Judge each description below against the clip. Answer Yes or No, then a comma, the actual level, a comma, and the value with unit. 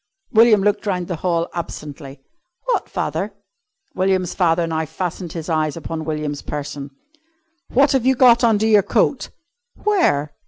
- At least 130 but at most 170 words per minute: Yes, average, 145 wpm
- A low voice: No, medium, 175 Hz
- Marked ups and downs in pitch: Yes, wide, 5.9 semitones